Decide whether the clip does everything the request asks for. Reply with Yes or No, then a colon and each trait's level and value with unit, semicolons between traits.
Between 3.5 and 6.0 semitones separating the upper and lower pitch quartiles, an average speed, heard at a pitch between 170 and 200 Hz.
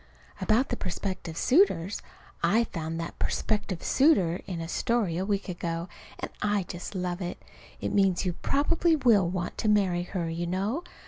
Yes: average, 3.8 semitones; average, 170 wpm; high, 190 Hz